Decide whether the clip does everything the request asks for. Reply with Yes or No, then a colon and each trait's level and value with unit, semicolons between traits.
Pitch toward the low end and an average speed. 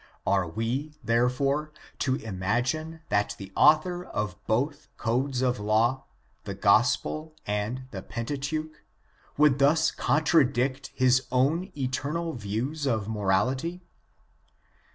No: low, 130 Hz; slow, 110 wpm